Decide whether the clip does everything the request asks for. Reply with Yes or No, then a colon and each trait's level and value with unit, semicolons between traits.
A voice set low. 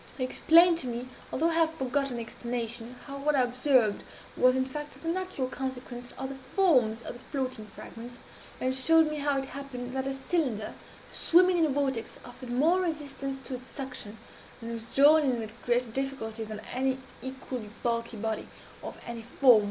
No: very high, 260 Hz